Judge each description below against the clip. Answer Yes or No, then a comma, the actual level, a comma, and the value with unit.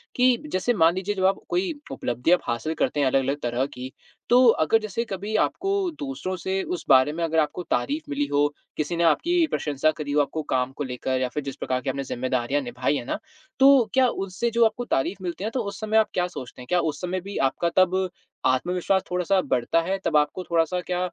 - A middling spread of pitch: No, wide, 6.1 semitones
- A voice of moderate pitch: Yes, medium, 170 Hz